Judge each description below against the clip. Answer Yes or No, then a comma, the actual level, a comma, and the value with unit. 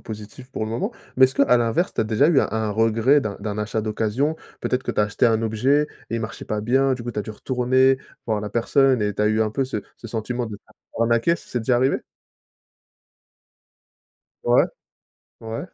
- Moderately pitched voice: No, low, 115 Hz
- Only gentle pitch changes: No, average, 3.2 semitones